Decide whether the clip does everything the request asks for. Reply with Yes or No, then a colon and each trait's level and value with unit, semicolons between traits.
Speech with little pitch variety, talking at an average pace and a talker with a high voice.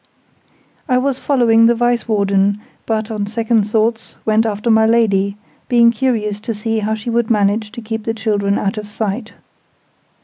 Yes: narrow, 1.8 semitones; average, 170 wpm; high, 220 Hz